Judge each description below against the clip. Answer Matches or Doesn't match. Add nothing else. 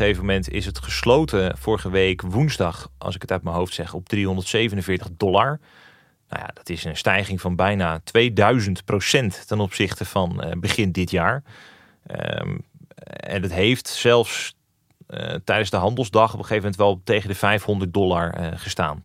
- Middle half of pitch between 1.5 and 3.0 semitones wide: Matches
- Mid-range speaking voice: Doesn't match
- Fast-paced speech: Doesn't match